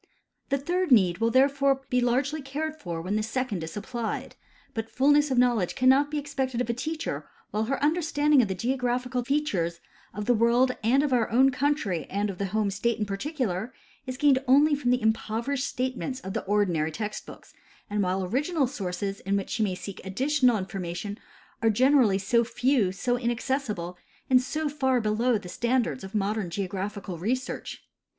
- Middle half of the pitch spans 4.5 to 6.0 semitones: Yes, average, 5.1 semitones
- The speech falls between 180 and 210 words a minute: Yes, average, 185 wpm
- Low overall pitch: No, high, 240 Hz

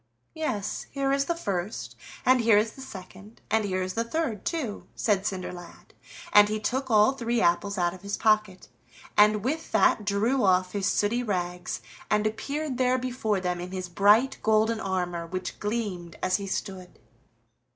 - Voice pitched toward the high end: Yes, high, 210 Hz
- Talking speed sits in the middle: Yes, average, 170 wpm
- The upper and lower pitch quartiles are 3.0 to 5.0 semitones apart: Yes, average, 4.2 semitones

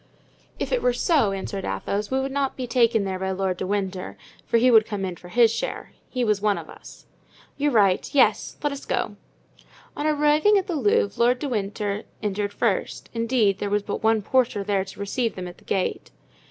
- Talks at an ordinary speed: No, fast, 210 wpm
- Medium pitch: No, high, 215 Hz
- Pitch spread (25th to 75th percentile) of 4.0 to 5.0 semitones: Yes, average, 4.5 semitones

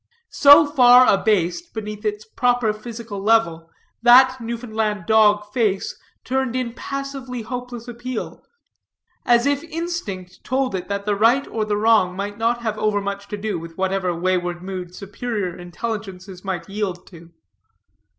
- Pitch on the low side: No, high, 215 Hz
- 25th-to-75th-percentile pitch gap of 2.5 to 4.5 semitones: Yes, average, 4.0 semitones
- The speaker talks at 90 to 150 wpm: Yes, average, 140 wpm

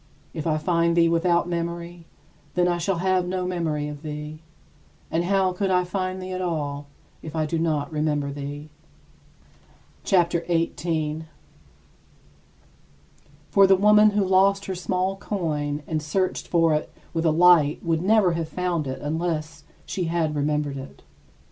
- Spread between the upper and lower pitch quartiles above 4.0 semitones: No, average, 3.0 semitones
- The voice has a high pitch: No, medium, 170 Hz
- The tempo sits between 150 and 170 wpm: Yes, average, 155 wpm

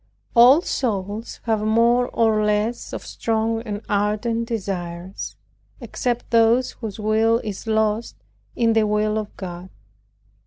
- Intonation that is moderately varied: No, narrow, 1.8 semitones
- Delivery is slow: Yes, slow, 125 wpm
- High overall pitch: Yes, high, 220 Hz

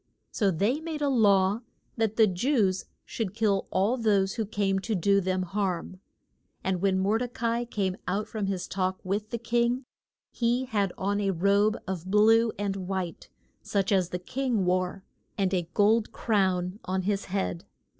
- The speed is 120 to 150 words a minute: No, average, 175 wpm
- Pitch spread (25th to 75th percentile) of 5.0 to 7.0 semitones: No, average, 3.0 semitones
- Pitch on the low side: No, high, 200 Hz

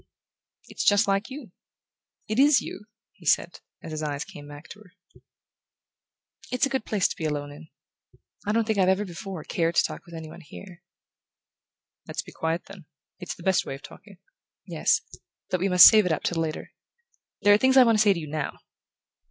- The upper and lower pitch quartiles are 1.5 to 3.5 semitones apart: No, average, 4.5 semitones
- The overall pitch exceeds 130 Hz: Yes, medium, 185 Hz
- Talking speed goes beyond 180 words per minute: Yes, fast, 205 wpm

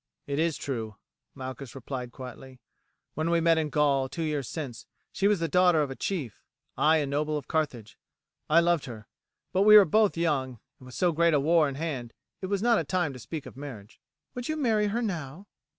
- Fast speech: Yes, fast, 215 wpm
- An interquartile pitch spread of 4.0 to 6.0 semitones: Yes, average, 4.5 semitones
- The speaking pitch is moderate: Yes, medium, 155 Hz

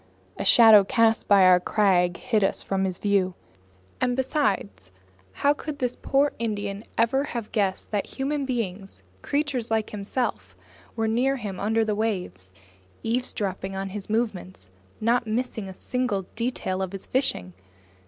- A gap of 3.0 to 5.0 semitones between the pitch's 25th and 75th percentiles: Yes, average, 4.3 semitones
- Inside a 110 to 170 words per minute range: Yes, average, 150 wpm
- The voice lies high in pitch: Yes, high, 215 Hz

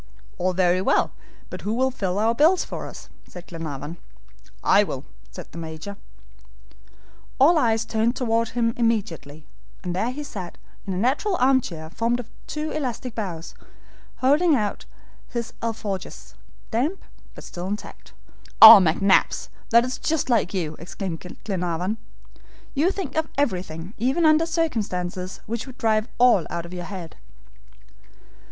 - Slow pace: No, average, 145 wpm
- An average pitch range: No, wide, 6.1 semitones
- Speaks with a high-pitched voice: Yes, high, 220 Hz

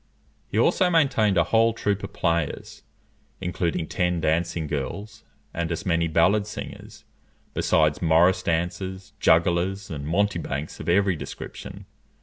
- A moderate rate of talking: No, slow, 130 wpm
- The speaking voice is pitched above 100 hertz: No, very low, 90 Hz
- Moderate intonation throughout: Yes, average, 3.2 semitones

